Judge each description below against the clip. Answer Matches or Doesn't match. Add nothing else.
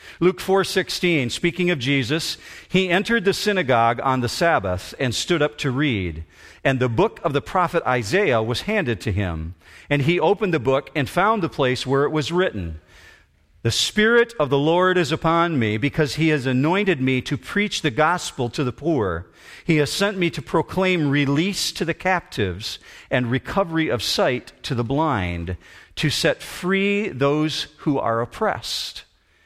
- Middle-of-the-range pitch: Matches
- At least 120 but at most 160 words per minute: Doesn't match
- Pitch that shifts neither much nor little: Doesn't match